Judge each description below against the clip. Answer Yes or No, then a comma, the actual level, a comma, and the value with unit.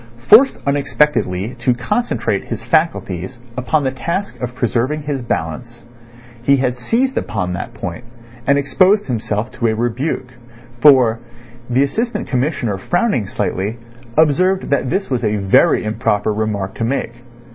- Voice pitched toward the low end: Yes, low, 125 Hz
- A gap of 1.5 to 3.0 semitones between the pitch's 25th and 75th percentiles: No, average, 5.2 semitones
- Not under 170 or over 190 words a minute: No, average, 140 wpm